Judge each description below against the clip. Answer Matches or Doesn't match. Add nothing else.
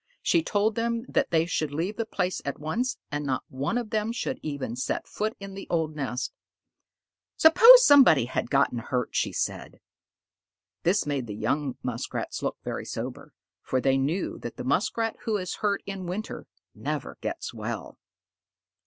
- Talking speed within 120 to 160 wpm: Doesn't match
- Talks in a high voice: Doesn't match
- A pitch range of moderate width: Doesn't match